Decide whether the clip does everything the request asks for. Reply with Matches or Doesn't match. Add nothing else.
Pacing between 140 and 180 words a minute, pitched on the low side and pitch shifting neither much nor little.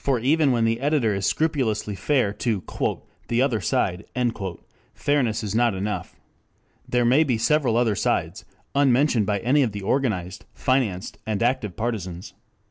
Matches